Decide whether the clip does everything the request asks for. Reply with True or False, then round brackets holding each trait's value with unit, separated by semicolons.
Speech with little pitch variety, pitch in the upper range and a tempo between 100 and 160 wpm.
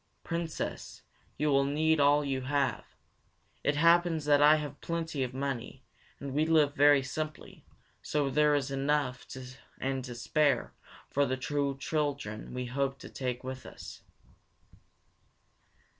False (2.1 semitones; 140 Hz; 140 wpm)